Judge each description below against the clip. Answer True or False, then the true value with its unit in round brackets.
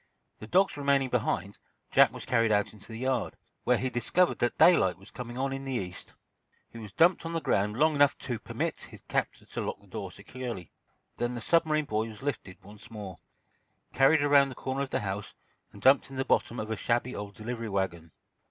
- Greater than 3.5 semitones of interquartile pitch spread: True (4.5 semitones)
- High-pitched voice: False (120 Hz)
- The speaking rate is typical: False (210 wpm)